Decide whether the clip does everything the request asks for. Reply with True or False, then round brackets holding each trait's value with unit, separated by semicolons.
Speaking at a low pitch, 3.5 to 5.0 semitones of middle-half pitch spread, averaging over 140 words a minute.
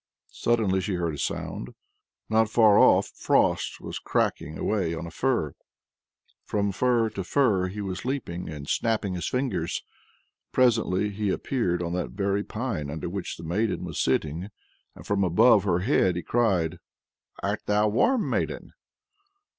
True (100 Hz; 4.4 semitones; 155 wpm)